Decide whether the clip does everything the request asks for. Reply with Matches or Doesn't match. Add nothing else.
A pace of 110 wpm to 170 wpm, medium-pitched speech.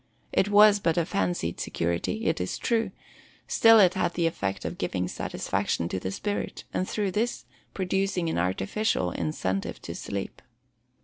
Matches